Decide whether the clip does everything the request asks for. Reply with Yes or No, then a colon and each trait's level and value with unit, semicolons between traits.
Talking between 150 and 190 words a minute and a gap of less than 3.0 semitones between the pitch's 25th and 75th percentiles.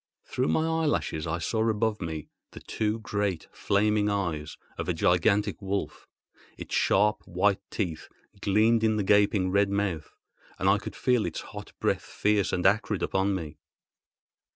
Yes: average, 155 wpm; narrow, 2.5 semitones